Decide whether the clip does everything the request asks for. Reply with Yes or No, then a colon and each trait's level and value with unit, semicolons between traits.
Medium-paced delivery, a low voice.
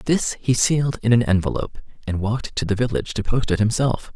No: fast, 215 wpm; low, 115 Hz